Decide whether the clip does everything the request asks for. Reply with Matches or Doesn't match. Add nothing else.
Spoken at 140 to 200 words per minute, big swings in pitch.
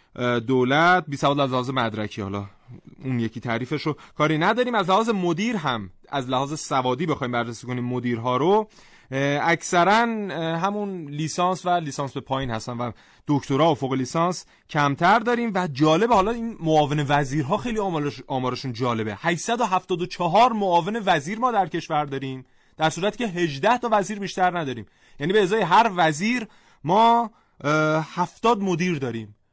Matches